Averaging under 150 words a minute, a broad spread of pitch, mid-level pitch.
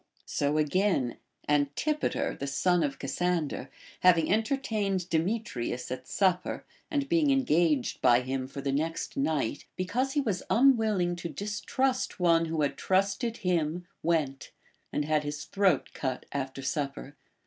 Yes: slow, 135 wpm; wide, 6.2 semitones; medium, 170 Hz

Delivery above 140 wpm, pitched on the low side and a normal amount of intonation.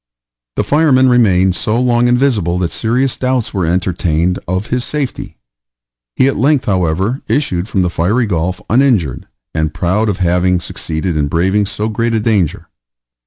No: average, 160 wpm; low, 100 Hz; wide, 5.7 semitones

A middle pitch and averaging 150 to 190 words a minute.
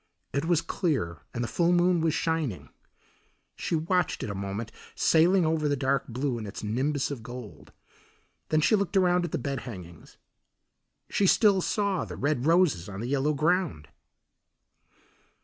Yes: medium, 145 Hz; average, 165 wpm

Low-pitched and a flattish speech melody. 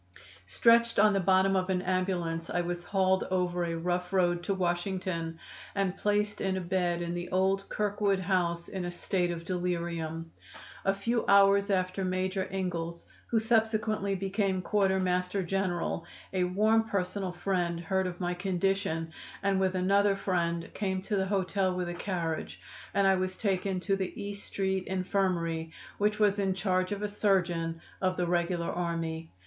No: medium, 185 Hz; narrow, 2.0 semitones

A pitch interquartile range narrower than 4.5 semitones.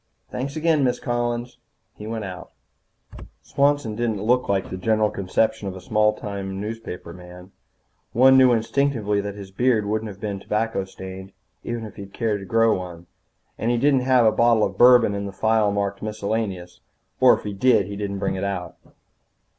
Yes: average, 3.2 semitones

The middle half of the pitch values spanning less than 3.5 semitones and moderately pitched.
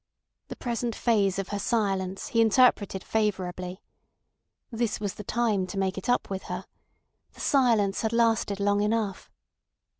No: average, 2.9 semitones; high, 205 Hz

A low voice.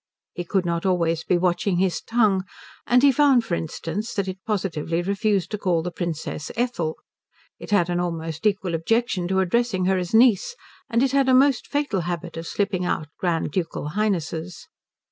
No: medium, 185 Hz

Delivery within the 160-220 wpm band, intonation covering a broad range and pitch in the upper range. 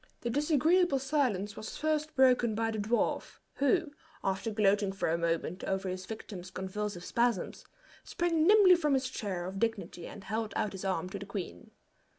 Yes: average, 170 wpm; wide, 6.2 semitones; high, 215 Hz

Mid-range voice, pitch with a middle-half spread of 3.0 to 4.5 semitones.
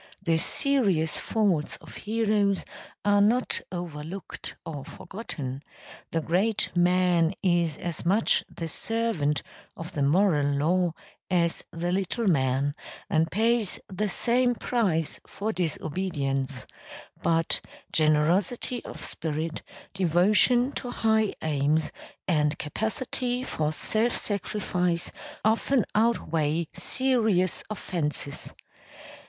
No: medium, 180 Hz; wide, 5.5 semitones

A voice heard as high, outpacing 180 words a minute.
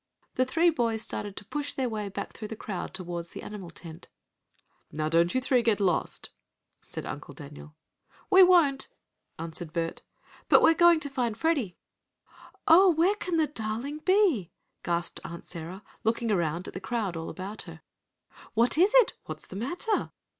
No: high, 220 Hz; average, 170 wpm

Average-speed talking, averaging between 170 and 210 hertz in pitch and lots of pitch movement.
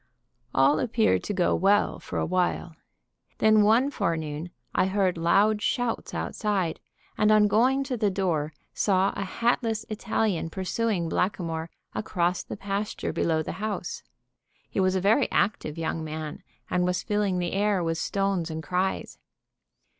No: average, 150 wpm; high, 190 Hz; average, 4.0 semitones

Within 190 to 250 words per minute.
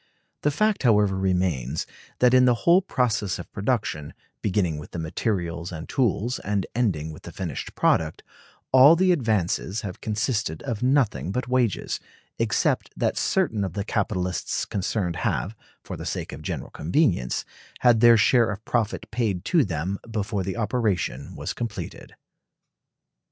No: average, 150 wpm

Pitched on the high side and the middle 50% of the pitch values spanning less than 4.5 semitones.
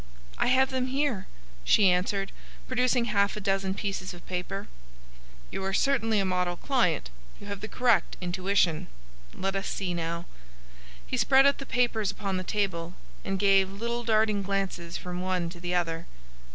Yes: high, 195 Hz; average, 3.7 semitones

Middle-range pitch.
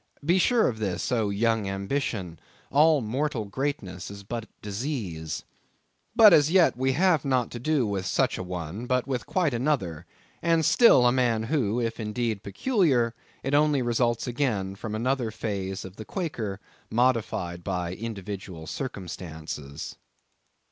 No: low, 115 Hz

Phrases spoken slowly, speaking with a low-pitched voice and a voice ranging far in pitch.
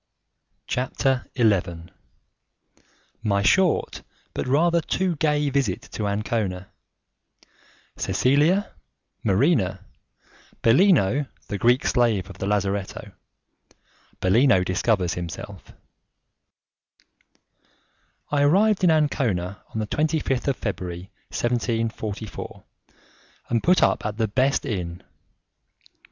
Yes: slow, 90 wpm; low, 115 Hz; wide, 6.5 semitones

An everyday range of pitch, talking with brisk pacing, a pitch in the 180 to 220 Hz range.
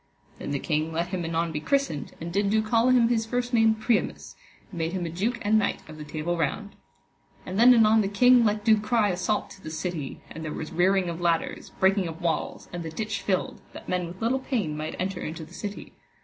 Yes: average, 5.0 semitones; fast, 235 wpm; medium, 185 Hz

